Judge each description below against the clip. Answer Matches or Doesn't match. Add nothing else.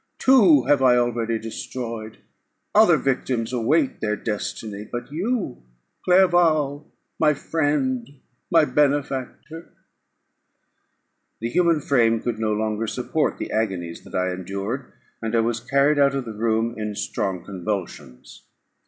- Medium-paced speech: Doesn't match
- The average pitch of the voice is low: Matches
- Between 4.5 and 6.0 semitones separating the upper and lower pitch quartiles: Matches